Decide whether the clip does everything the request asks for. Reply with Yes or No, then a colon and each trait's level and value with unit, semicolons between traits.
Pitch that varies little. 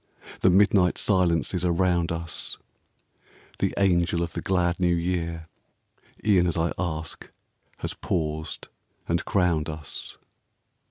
Yes: narrow, 1.6 semitones